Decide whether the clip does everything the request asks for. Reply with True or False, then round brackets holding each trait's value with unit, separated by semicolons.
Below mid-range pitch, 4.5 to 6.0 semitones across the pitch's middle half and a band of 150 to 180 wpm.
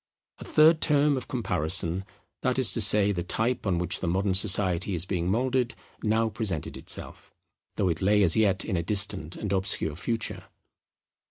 False (100 Hz; 4.0 semitones; 170 wpm)